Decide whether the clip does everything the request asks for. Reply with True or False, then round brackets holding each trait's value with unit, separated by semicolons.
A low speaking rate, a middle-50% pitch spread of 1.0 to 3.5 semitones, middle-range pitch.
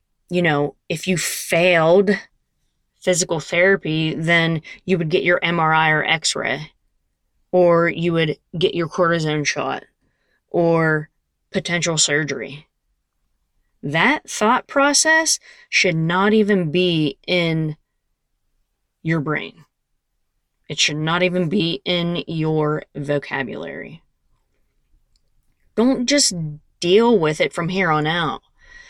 True (110 wpm; 3.0 semitones; 170 Hz)